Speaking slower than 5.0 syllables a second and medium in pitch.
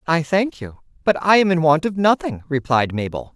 No: 5.2 syllables/s; medium, 160 Hz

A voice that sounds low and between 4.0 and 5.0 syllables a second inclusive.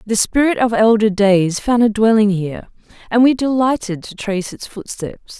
No: high, 215 Hz; 4.9 syllables/s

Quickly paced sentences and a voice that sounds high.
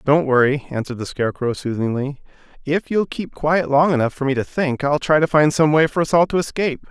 No: fast, 235 wpm; medium, 145 Hz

